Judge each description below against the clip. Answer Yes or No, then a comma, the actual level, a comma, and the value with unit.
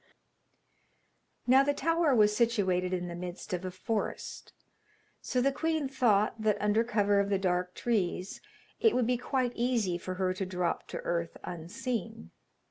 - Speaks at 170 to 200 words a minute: No, average, 160 wpm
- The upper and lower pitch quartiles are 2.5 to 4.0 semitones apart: No, average, 5.2 semitones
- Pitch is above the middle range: Yes, high, 205 Hz